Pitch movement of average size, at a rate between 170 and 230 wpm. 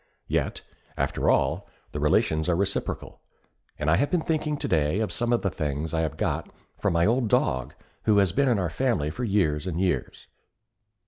No: wide, 7.3 semitones; average, 190 wpm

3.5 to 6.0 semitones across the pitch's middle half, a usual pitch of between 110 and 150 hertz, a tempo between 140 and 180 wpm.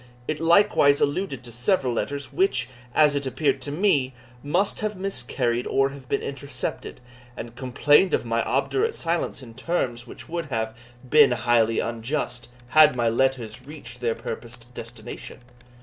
Yes: average, 4.2 semitones; low, 135 Hz; average, 150 wpm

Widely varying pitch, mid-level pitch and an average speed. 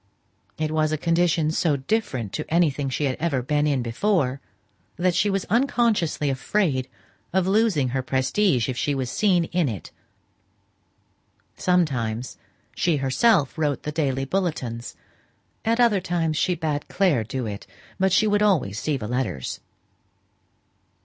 Yes: wide, 5.7 semitones; medium, 155 Hz; average, 145 wpm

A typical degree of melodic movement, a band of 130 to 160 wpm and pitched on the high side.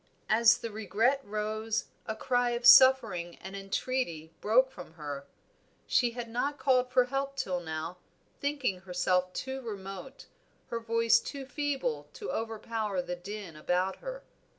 No: wide, 5.8 semitones; average, 145 wpm; high, 225 Hz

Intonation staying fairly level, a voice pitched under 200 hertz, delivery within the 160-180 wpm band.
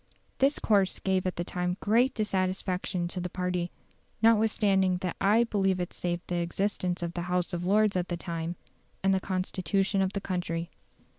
Yes: narrow, 2.0 semitones; medium, 185 Hz; average, 175 wpm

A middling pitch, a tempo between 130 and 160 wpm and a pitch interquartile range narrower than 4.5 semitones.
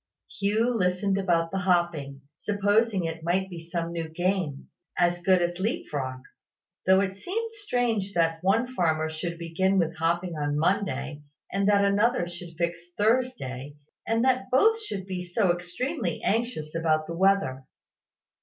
Yes: medium, 180 Hz; average, 150 wpm; average, 3.6 semitones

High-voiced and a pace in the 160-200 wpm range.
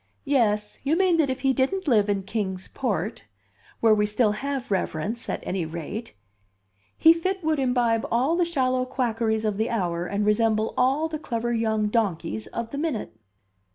Yes: high, 230 Hz; average, 175 wpm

